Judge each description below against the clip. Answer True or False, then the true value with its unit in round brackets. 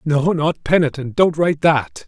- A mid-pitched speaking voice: True (150 Hz)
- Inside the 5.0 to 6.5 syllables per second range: False (4.6 syllables/s)